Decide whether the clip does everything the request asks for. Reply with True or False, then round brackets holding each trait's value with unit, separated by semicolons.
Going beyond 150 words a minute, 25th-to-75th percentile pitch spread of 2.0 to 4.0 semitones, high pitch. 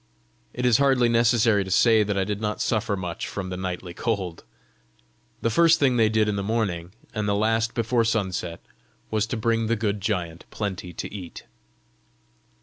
False (180 wpm; 3.3 semitones; 105 Hz)